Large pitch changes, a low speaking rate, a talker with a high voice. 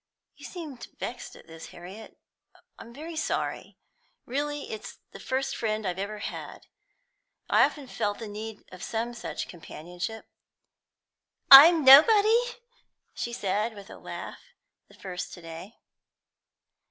Yes: wide, 5.9 semitones; slow, 130 wpm; high, 225 Hz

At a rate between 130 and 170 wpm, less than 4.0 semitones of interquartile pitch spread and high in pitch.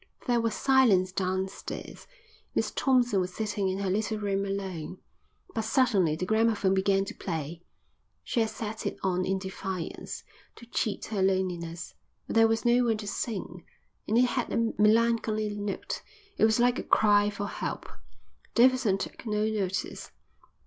Yes: average, 160 wpm; average, 3.1 semitones; high, 205 Hz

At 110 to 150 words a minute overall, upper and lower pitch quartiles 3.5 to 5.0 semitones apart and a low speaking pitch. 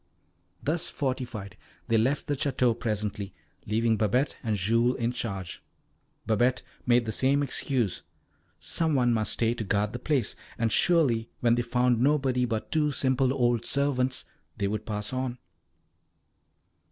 No: average, 145 wpm; average, 3.0 semitones; low, 120 Hz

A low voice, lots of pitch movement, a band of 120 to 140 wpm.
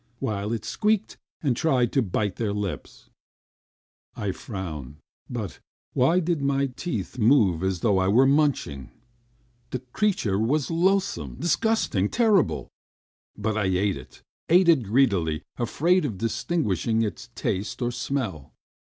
Yes: low, 115 Hz; wide, 7.3 semitones; slow, 135 wpm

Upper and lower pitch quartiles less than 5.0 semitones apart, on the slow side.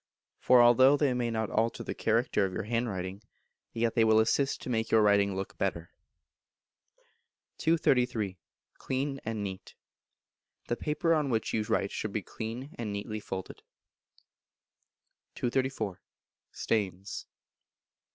Yes: average, 3.6 semitones; slow, 130 wpm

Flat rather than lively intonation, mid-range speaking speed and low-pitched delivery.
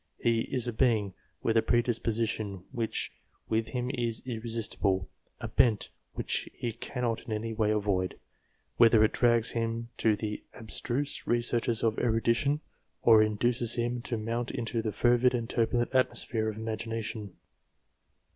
Yes: narrow, 1.6 semitones; average, 145 wpm; low, 115 Hz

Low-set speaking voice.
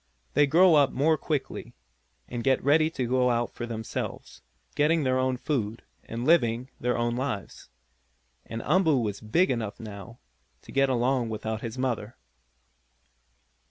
Yes: low, 125 Hz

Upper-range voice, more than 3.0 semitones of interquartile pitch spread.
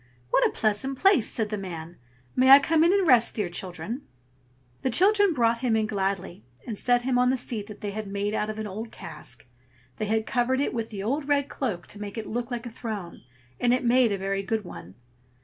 Yes: high, 225 Hz; average, 4.0 semitones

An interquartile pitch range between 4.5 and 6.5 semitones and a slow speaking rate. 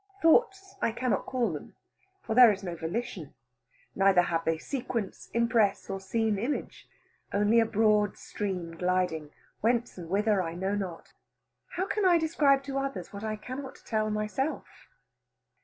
No: average, 5.0 semitones; average, 155 wpm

